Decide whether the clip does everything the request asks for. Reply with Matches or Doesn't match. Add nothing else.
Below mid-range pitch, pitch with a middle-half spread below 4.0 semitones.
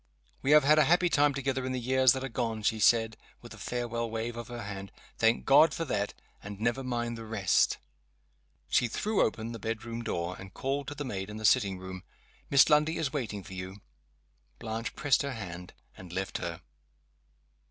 Doesn't match